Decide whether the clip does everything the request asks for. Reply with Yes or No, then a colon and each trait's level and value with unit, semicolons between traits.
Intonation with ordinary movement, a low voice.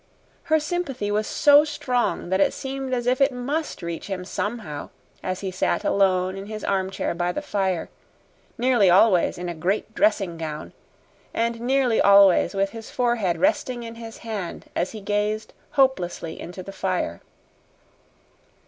No: average, 5.0 semitones; high, 205 Hz